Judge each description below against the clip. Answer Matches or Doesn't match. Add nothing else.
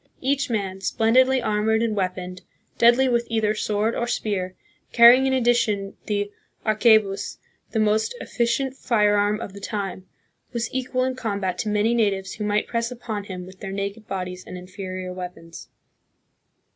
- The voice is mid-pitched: Doesn't match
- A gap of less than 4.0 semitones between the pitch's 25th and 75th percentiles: Matches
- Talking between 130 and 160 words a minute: Matches